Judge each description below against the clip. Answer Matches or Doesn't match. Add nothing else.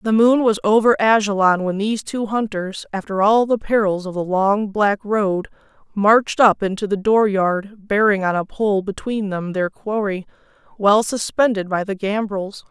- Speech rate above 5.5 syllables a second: Doesn't match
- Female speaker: Matches